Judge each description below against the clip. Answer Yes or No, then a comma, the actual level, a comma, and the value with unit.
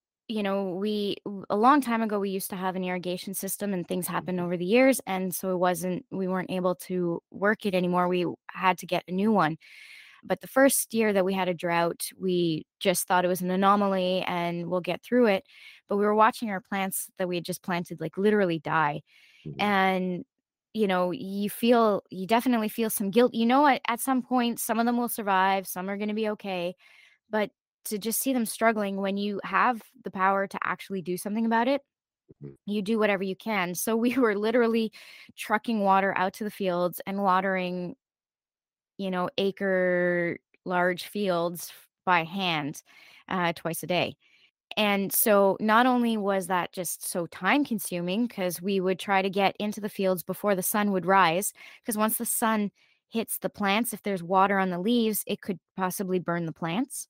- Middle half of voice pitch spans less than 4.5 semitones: Yes, average, 3.3 semitones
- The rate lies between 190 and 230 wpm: Yes, average, 195 wpm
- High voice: Yes, high, 195 Hz